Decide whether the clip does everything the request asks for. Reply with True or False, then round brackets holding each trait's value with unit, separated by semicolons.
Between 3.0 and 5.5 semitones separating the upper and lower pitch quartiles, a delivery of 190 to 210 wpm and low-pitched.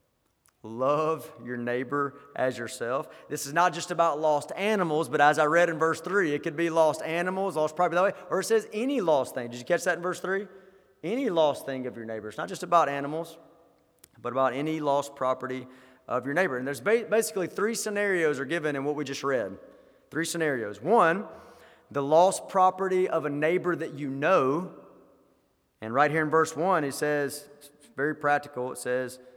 False (4.2 semitones; 200 wpm; 155 Hz)